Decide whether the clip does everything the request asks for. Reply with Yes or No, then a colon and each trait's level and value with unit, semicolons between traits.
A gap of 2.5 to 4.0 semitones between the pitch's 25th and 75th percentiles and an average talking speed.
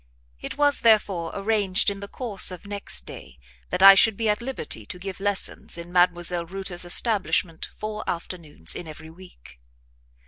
Yes: average, 3.3 semitones; average, 165 wpm